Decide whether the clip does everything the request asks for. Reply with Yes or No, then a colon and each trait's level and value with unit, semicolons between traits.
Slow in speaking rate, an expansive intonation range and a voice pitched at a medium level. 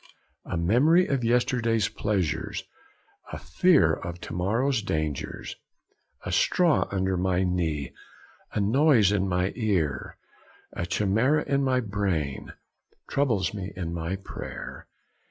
No: slow, 120 wpm; wide, 5.7 semitones; low, 100 Hz